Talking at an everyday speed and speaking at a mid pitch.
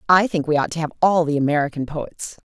No: fast, 240 wpm; medium, 160 Hz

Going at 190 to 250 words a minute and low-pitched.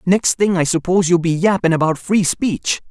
No: fast, 205 wpm; medium, 175 Hz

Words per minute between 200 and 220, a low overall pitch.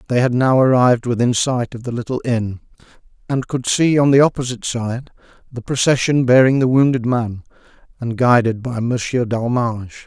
No: average, 165 wpm; low, 125 Hz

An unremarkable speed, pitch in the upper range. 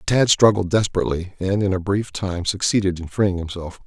No: average, 185 wpm; very low, 95 Hz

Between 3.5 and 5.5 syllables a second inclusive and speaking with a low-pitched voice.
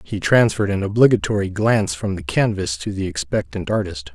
No: 5.7 syllables/s; very low, 95 Hz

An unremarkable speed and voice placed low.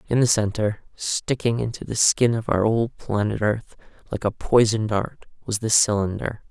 Yes: average, 175 wpm; low, 110 Hz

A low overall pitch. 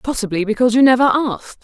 No: high, 240 Hz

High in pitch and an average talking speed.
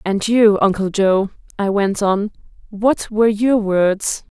Yes: high, 205 Hz; average, 150 wpm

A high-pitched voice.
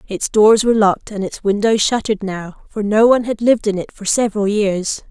Yes: high, 210 Hz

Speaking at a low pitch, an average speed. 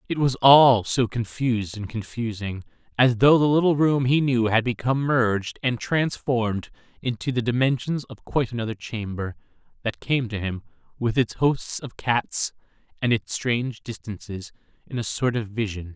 Yes: low, 120 Hz; average, 165 wpm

